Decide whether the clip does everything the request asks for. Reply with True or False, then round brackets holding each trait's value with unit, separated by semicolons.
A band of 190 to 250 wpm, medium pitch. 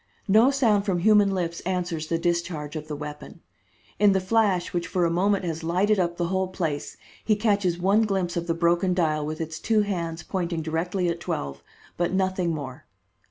True (195 wpm; 175 Hz)